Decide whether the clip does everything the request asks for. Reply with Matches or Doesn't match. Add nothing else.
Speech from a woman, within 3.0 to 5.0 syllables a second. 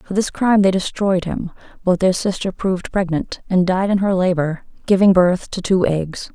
Matches